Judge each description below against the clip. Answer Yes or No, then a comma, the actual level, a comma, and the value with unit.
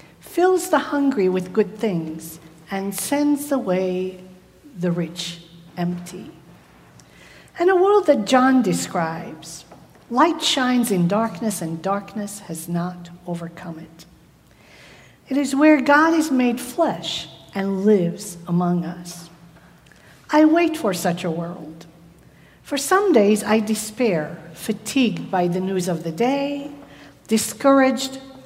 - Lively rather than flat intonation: Yes, wide, 7.6 semitones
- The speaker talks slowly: Yes, slow, 120 wpm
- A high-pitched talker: Yes, high, 195 Hz